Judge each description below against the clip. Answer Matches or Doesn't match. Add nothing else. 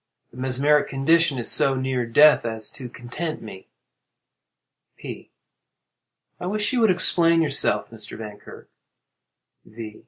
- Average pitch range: Doesn't match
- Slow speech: Matches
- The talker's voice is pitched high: Doesn't match